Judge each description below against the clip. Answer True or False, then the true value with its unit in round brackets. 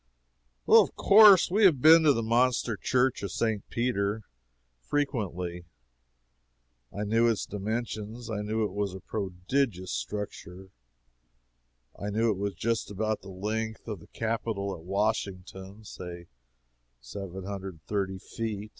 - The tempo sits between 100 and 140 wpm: True (135 wpm)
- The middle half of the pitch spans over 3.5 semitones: False (3.1 semitones)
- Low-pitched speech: True (105 Hz)